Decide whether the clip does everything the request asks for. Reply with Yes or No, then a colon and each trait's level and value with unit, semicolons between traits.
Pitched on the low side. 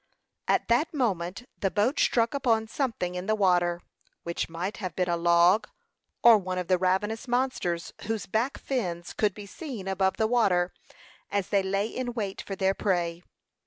No: high, 195 Hz